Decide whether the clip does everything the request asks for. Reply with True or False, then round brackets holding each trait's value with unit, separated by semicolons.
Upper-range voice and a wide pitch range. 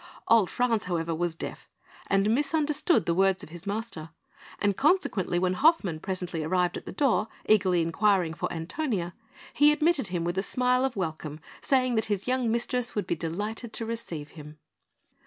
True (200 Hz; 6.3 semitones)